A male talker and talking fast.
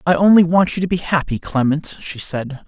Yes: male; fast, 225 wpm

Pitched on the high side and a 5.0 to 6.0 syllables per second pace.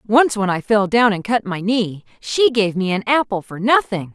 No: high, 210 Hz; 4.6 syllables/s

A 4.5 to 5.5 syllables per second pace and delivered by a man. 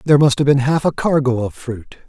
No: 5.8 syllables/s; male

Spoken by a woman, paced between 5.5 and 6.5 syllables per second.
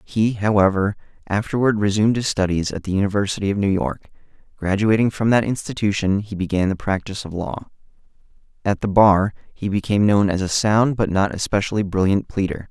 No: male; 5.8 syllables/s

